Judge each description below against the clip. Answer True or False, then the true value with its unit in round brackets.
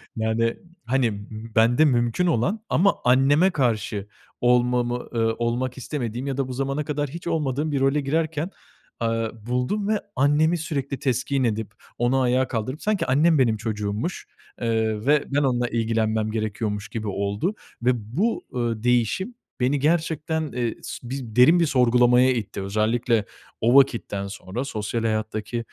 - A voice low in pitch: True (125 Hz)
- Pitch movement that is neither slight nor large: True (4.3 semitones)